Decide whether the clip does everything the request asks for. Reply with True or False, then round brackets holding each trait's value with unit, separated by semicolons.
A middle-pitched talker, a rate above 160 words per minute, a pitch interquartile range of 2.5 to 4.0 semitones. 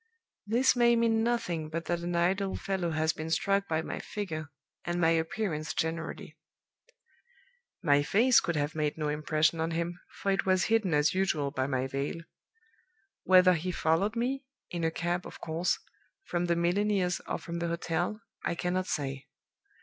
True (170 Hz; 170 wpm; 3.4 semitones)